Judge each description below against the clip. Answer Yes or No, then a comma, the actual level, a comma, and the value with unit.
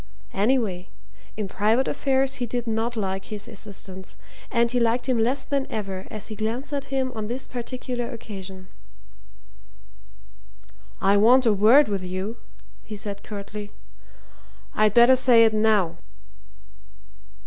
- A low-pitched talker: No, high, 220 Hz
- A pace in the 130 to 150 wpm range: Yes, slow, 135 wpm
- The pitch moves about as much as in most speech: Yes, average, 3.5 semitones